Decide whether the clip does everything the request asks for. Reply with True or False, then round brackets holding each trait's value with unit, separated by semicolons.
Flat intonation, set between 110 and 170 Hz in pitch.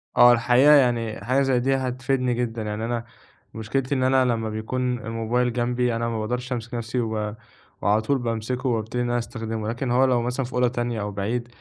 True (2.0 semitones; 120 Hz)